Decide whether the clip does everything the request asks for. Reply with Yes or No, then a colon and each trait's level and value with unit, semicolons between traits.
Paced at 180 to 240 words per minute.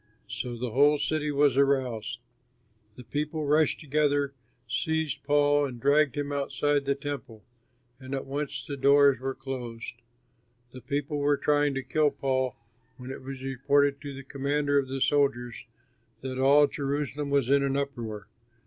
No: average, 160 wpm